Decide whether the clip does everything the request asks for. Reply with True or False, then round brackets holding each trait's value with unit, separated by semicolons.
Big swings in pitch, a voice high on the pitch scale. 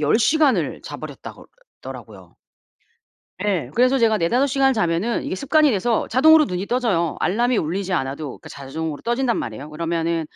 True (7.2 semitones; 200 Hz)